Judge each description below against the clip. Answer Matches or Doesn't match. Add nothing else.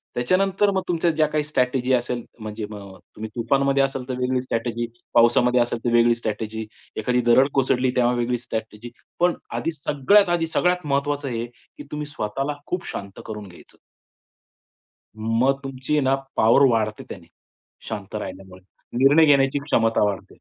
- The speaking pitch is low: Matches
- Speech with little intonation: Doesn't match